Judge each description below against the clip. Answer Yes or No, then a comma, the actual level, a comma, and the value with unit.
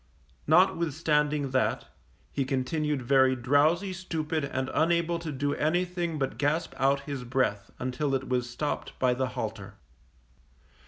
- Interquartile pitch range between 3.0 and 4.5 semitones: Yes, average, 3.4 semitones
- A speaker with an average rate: No, slow, 130 wpm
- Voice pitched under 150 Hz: Yes, medium, 140 Hz